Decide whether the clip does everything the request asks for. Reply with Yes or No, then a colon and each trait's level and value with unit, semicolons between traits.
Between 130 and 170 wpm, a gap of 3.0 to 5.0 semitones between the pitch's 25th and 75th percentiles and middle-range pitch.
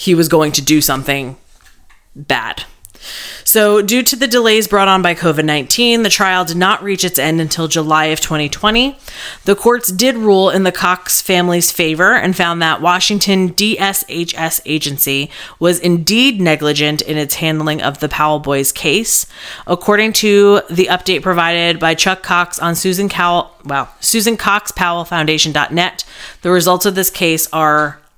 Yes: average, 160 wpm; average, 4.2 semitones; medium, 175 Hz